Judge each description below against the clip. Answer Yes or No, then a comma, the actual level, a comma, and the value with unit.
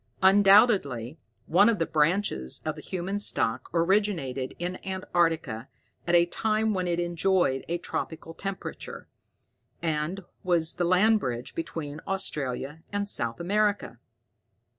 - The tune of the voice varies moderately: Yes, average, 4.5 semitones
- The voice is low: No, medium, 175 Hz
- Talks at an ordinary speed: No, slow, 125 wpm